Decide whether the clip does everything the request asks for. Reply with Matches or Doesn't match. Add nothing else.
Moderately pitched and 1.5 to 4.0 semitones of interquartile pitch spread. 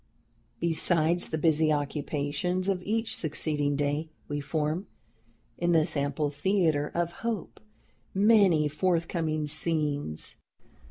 Matches